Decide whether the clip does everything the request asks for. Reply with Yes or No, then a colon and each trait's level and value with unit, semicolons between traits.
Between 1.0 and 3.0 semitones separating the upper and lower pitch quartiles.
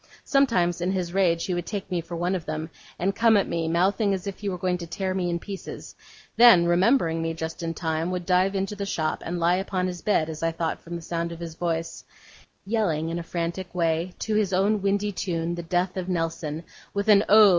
Yes: average, 2.7 semitones